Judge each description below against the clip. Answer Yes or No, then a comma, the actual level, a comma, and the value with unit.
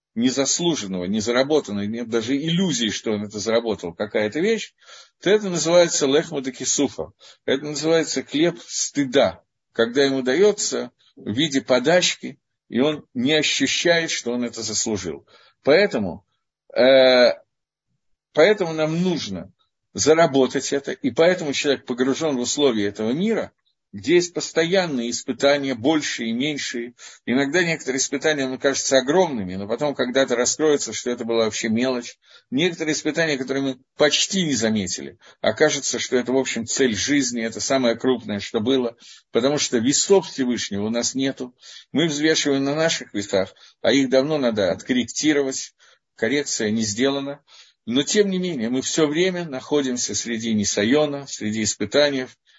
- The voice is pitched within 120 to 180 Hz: Yes, low, 135 Hz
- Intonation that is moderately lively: Yes, average, 4.5 semitones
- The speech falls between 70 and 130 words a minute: No, average, 140 wpm